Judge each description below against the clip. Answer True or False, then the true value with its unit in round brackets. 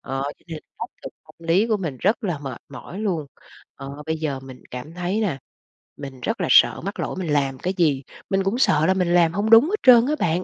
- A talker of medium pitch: True (170 Hz)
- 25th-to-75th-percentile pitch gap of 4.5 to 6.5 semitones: True (5.6 semitones)